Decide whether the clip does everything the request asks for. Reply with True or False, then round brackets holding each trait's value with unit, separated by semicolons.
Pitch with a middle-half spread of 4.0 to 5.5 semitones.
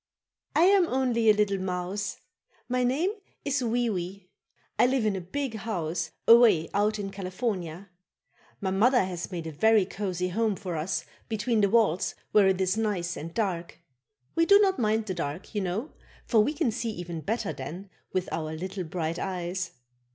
True (4.3 semitones)